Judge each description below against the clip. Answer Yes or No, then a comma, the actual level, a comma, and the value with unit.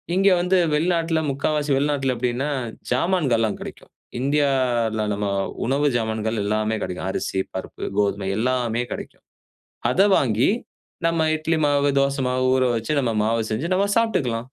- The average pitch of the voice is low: Yes, low, 130 Hz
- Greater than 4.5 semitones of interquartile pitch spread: Yes, average, 4.9 semitones